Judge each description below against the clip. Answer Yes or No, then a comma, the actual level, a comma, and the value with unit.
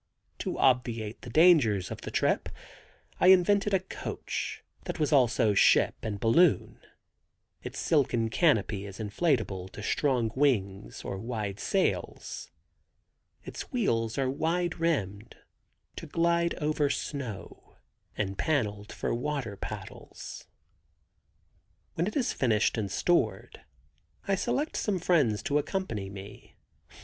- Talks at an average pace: No, slow, 120 wpm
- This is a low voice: Yes, low, 125 Hz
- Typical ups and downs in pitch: No, wide, 8.1 semitones